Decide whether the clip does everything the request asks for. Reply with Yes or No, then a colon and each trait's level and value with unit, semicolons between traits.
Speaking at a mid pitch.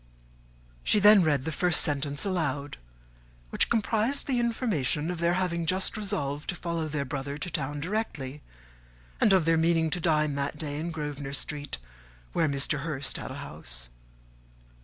Yes: medium, 155 Hz